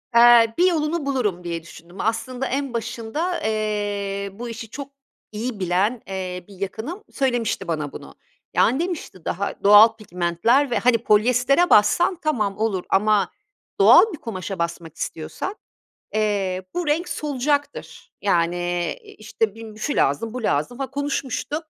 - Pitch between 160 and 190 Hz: No, high, 220 Hz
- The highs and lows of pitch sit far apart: Yes, wide, 5.7 semitones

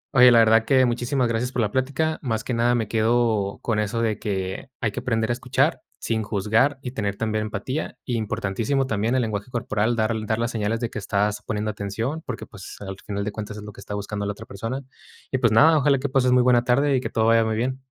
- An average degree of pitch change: Yes, average, 3.0 semitones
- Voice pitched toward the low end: Yes, low, 115 Hz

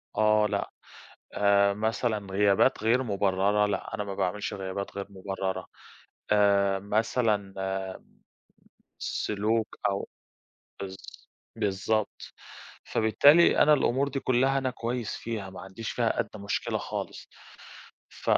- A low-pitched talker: Yes, low, 105 Hz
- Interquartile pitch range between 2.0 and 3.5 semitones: Yes, narrow, 2.5 semitones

